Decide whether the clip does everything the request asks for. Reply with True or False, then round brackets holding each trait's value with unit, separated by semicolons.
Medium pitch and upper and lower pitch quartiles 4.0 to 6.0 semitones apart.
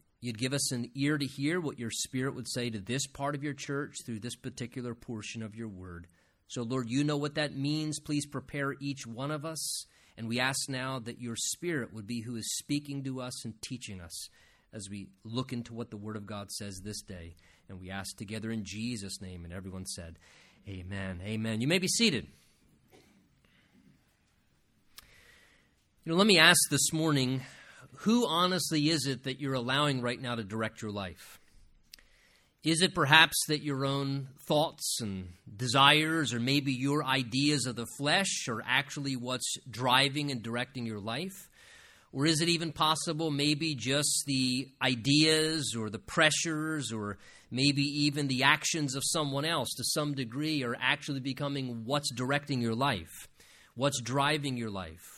False (130 Hz; 4.6 semitones)